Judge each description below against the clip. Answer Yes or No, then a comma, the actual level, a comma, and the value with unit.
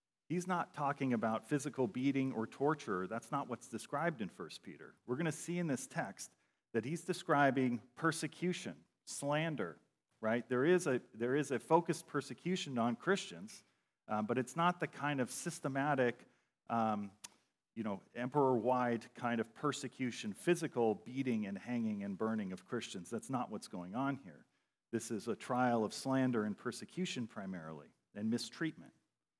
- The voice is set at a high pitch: No, low, 135 Hz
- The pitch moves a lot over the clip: Yes, wide, 5.9 semitones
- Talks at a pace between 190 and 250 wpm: No, average, 160 wpm